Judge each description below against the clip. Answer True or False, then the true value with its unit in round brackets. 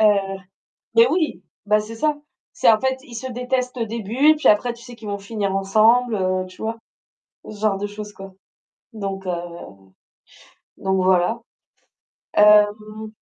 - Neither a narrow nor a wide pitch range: True (3.0 semitones)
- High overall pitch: True (215 Hz)